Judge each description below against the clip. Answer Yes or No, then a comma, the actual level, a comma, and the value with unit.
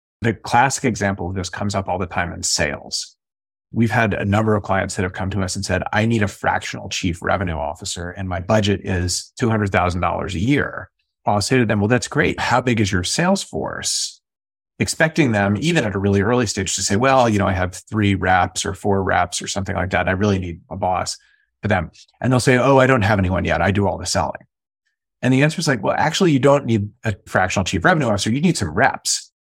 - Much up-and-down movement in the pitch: No, average, 4.1 semitones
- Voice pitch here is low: Yes, low, 100 Hz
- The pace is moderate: No, fast, 235 wpm